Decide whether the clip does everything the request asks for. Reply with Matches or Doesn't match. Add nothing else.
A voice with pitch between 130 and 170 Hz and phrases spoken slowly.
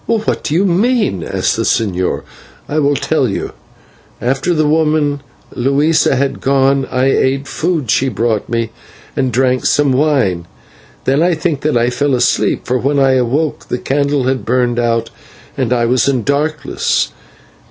Doesn't match